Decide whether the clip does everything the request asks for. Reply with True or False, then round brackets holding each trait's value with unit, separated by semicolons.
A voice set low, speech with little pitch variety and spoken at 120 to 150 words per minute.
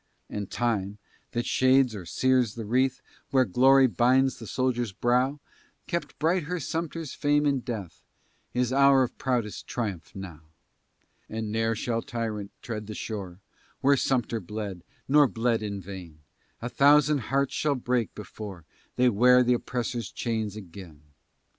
False (120 Hz; 3.9 semitones; 145 wpm)